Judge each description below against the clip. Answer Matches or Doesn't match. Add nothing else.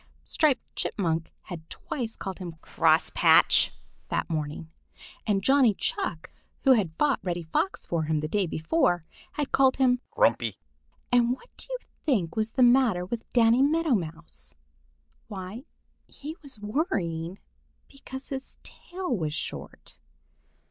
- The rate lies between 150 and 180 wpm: Doesn't match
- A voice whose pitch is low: Doesn't match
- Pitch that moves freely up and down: Matches